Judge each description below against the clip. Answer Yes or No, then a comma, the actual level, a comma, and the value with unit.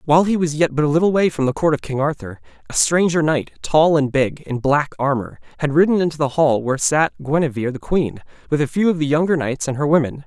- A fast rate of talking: Yes, fast, 250 wpm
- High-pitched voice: No, medium, 150 Hz